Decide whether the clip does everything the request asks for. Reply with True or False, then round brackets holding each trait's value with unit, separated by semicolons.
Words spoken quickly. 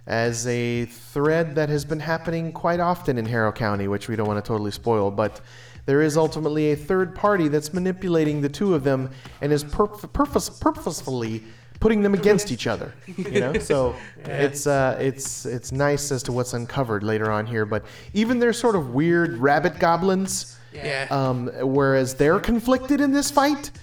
False (180 wpm)